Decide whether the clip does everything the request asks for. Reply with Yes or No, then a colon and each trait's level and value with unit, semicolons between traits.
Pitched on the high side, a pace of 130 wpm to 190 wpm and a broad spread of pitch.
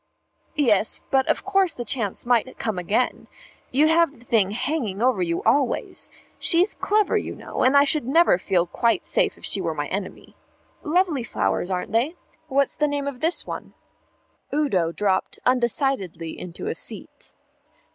Yes: very high, 250 Hz; average, 165 wpm; wide, 6.7 semitones